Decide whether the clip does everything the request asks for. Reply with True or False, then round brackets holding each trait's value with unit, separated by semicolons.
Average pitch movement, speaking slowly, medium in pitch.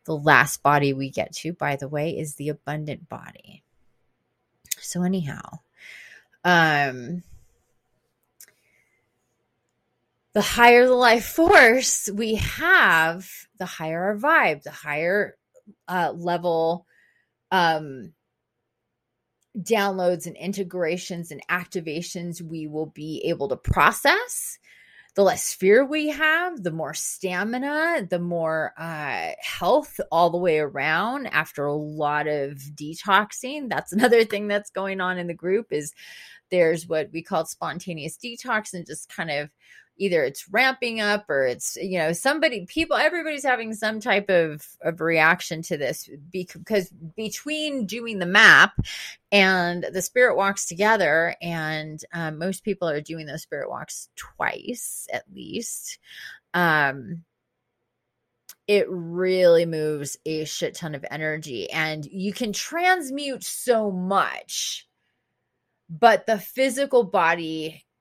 False (5.7 semitones; 125 wpm; 175 Hz)